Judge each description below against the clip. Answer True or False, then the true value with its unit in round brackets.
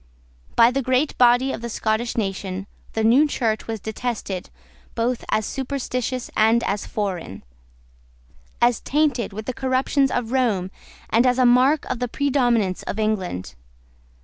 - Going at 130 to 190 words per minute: True (150 wpm)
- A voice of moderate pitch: False (235 Hz)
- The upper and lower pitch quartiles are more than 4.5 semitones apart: False (2.9 semitones)